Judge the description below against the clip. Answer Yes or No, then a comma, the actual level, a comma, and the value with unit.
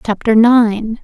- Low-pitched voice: No, high, 220 Hz